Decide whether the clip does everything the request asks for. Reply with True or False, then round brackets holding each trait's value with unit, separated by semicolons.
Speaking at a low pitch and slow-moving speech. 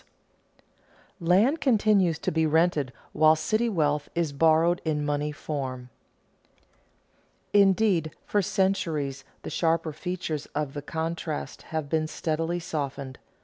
False (160 Hz; 120 wpm)